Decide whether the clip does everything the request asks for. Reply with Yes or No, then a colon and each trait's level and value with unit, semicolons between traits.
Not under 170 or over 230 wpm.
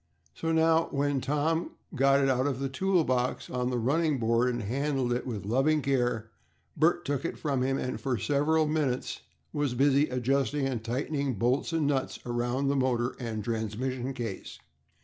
Yes: average, 175 wpm